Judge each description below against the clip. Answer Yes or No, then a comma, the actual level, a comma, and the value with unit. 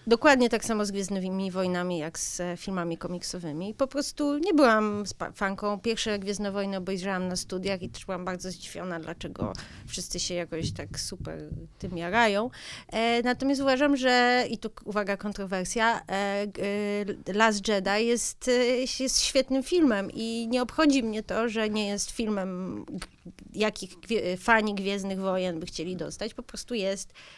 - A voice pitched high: Yes, high, 205 Hz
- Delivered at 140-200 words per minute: Yes, average, 150 wpm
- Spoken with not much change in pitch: No, average, 3.8 semitones